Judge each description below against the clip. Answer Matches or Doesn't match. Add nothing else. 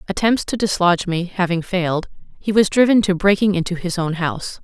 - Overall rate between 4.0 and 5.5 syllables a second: Doesn't match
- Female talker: Matches